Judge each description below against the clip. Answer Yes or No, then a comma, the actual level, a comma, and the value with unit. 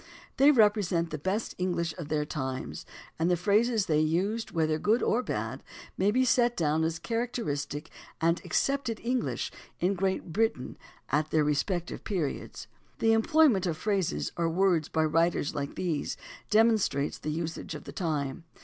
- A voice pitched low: No, medium, 175 Hz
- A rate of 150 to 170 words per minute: Yes, average, 160 wpm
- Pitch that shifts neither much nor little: No, wide, 5.8 semitones